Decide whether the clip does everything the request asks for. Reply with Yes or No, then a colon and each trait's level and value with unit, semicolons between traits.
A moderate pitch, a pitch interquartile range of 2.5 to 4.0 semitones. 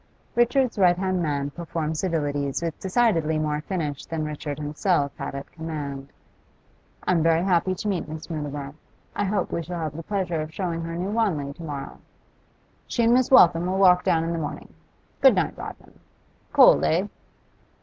Yes: medium, 165 Hz; average, 3.6 semitones